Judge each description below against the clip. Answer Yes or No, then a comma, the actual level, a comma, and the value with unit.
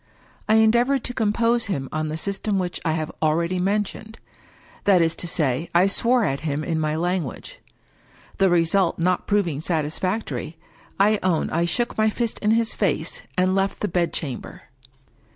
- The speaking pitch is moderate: Yes, medium, 180 Hz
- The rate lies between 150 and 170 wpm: No, average, 180 wpm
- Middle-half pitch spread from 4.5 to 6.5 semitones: Yes, average, 4.8 semitones